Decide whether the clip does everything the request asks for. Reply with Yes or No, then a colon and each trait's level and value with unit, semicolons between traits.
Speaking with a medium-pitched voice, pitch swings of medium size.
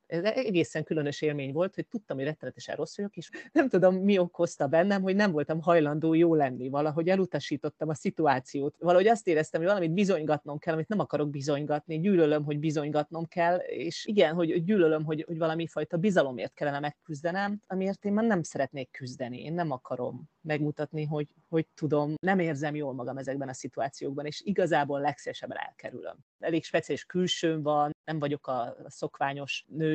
Yes: medium, 155 Hz; average, 3.1 semitones